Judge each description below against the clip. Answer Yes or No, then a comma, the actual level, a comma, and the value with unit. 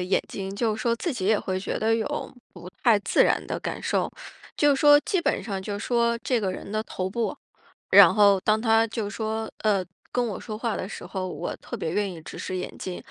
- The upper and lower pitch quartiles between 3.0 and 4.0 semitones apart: Yes, average, 3.4 semitones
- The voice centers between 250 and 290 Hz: No, high, 215 Hz